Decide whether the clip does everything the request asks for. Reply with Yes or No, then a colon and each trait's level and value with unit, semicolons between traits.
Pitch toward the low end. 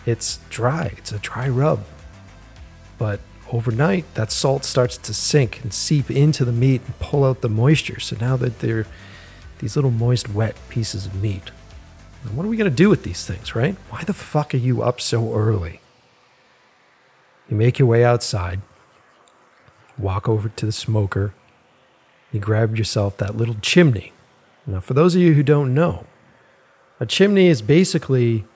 Yes: low, 115 Hz